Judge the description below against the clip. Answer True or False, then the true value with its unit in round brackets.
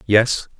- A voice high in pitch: False (110 Hz)